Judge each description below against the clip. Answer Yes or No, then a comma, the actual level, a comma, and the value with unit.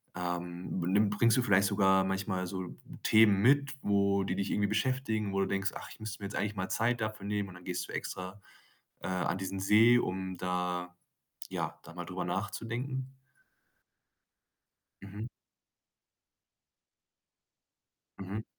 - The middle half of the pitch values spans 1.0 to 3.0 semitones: Yes, average, 2.7 semitones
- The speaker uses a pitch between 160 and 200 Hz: No, low, 100 Hz